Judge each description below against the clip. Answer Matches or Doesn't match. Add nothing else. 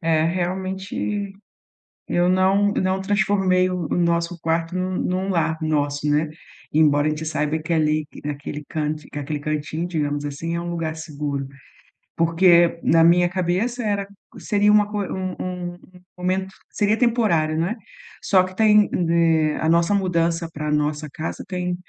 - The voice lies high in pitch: Doesn't match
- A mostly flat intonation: Doesn't match